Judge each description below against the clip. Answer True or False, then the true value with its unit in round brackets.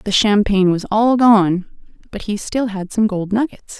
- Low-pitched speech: False (210 Hz)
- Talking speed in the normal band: True (190 wpm)